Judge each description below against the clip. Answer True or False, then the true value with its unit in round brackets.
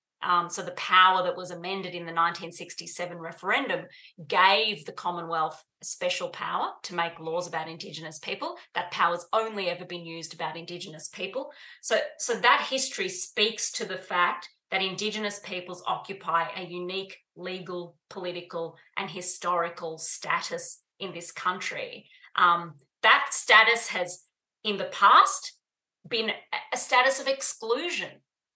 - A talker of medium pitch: True (180 Hz)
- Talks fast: False (140 wpm)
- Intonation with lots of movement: False (4.2 semitones)